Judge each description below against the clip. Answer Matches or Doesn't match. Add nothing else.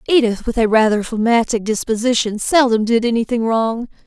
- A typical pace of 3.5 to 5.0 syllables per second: Doesn't match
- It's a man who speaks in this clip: Doesn't match